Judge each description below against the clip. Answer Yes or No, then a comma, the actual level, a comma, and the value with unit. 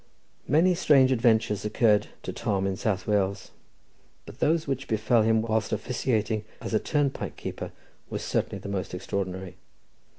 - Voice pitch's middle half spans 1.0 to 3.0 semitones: No, average, 4.2 semitones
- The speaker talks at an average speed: Yes, average, 145 wpm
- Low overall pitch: Yes, low, 110 Hz